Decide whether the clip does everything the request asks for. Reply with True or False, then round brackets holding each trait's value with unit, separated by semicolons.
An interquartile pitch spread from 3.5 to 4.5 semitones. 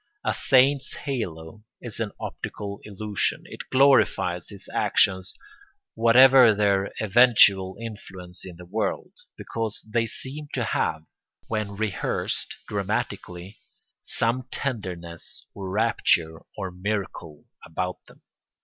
True (4.0 semitones)